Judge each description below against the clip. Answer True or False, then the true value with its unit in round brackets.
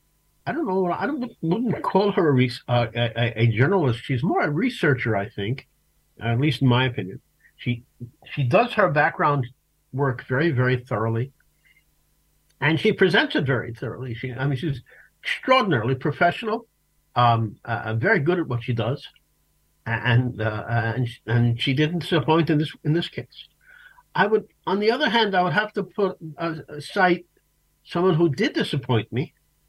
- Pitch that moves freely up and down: True (6.9 semitones)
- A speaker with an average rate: True (170 wpm)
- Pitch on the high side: False (140 Hz)